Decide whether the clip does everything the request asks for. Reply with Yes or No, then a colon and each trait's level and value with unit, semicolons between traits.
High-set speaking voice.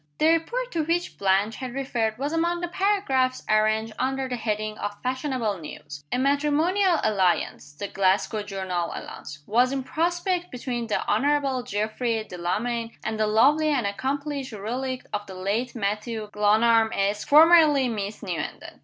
Yes: high, 240 Hz